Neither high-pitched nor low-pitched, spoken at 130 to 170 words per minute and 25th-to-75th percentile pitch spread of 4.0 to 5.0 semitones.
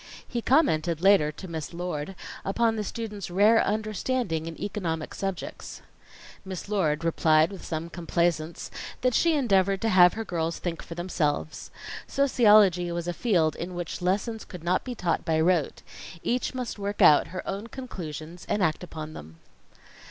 Yes: medium, 180 Hz; average, 160 wpm; average, 4.4 semitones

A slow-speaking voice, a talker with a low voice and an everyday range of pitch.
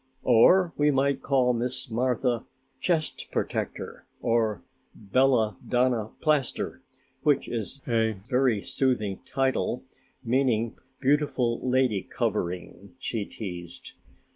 Yes: slow, 100 wpm; low, 125 Hz; average, 3.3 semitones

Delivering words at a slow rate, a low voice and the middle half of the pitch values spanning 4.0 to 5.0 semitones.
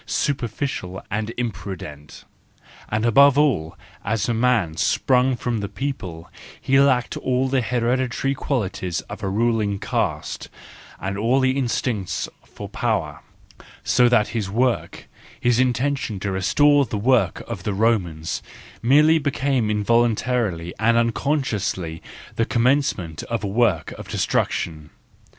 Yes: slow, 125 wpm; low, 115 Hz; average, 4.7 semitones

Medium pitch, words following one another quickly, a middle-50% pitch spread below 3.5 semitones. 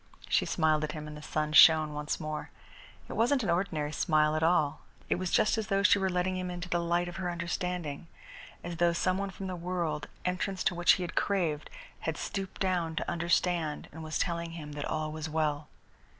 Yes: medium, 170 Hz; fast, 215 wpm; average, 2.9 semitones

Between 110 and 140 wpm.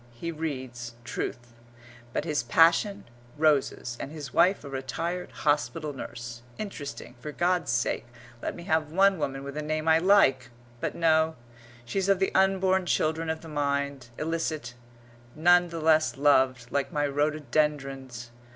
No: average, 150 wpm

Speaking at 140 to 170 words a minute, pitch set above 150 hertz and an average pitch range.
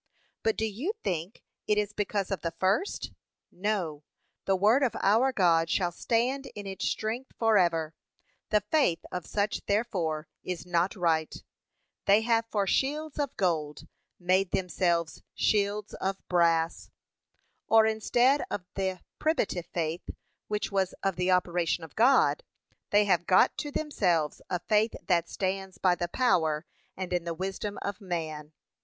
Yes: average, 150 wpm; high, 190 Hz; average, 3.9 semitones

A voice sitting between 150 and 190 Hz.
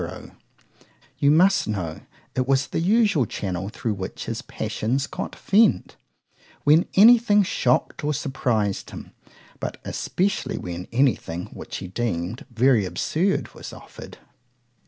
No: low, 130 Hz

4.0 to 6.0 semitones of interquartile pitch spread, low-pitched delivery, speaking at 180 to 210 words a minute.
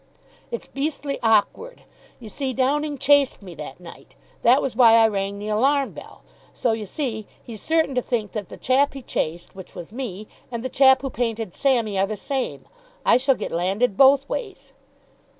No: average, 4.6 semitones; high, 245 Hz; average, 185 wpm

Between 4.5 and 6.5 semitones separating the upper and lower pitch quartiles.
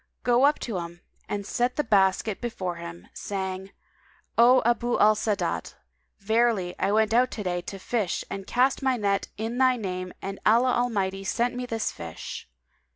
No: average, 4.1 semitones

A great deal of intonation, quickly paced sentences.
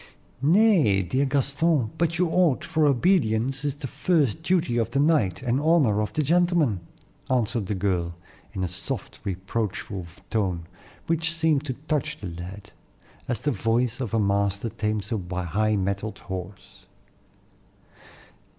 No: wide, 7.3 semitones; average, 145 wpm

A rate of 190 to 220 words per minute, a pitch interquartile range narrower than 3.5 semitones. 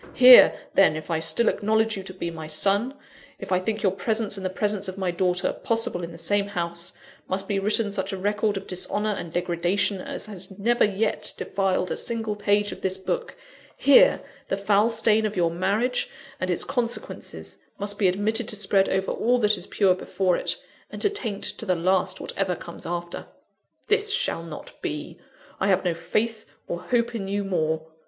Yes: average, 195 wpm; average, 3.1 semitones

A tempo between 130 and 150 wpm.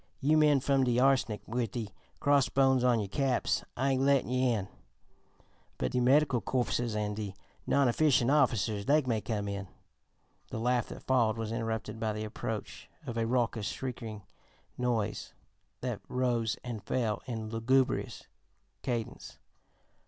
Yes: average, 145 wpm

